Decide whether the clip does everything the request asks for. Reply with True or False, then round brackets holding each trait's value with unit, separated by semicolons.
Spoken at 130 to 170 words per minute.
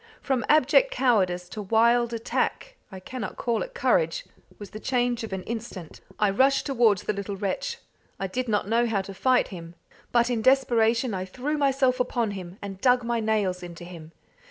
False (185 wpm)